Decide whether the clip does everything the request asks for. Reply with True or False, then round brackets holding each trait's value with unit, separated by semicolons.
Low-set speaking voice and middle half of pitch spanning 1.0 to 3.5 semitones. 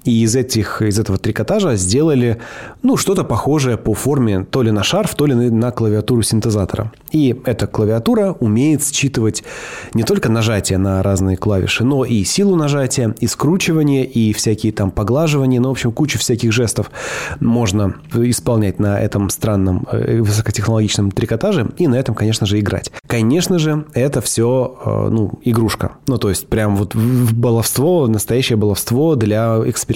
True (115 Hz; 3.2 semitones)